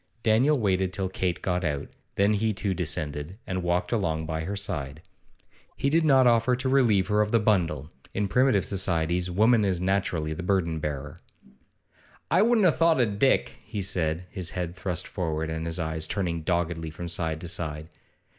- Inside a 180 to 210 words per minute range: Yes, average, 185 wpm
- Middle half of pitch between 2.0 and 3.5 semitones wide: No, average, 4.7 semitones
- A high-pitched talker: No, very low, 90 Hz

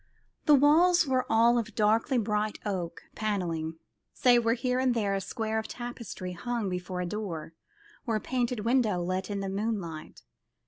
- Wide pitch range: No, average, 4.4 semitones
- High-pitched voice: Yes, high, 215 Hz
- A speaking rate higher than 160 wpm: Yes, average, 170 wpm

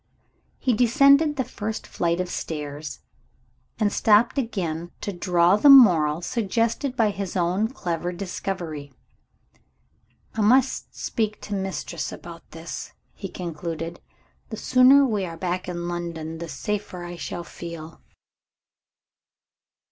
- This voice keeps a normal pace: No, slow, 125 wpm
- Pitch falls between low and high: Yes, medium, 180 Hz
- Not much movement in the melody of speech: No, average, 4.6 semitones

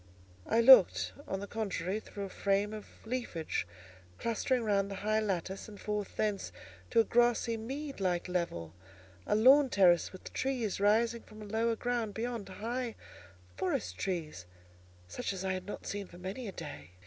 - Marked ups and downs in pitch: No, average, 3.7 semitones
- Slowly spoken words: No, average, 165 wpm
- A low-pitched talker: No, high, 205 Hz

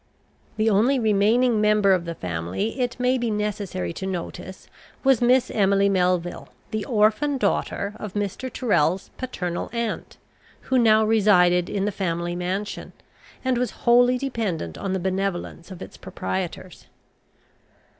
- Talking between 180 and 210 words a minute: No, average, 140 wpm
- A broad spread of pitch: No, average, 4.5 semitones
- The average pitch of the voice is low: No, high, 205 Hz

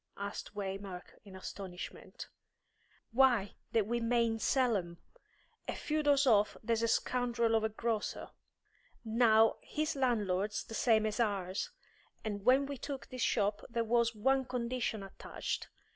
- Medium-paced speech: Yes, average, 145 wpm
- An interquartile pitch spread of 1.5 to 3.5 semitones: Yes, average, 3.1 semitones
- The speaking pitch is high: Yes, high, 225 Hz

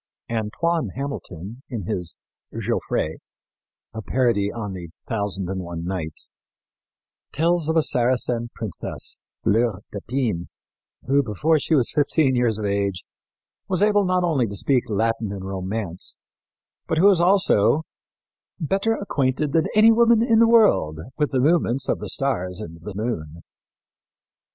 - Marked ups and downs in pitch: Yes, wide, 8.2 semitones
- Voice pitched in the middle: No, low, 120 Hz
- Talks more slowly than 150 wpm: Yes, average, 140 wpm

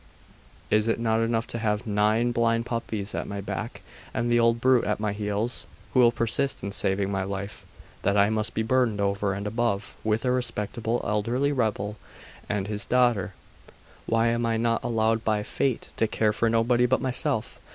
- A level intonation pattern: Yes, narrow, 2.2 semitones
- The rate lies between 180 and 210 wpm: Yes, average, 185 wpm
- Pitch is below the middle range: Yes, low, 115 Hz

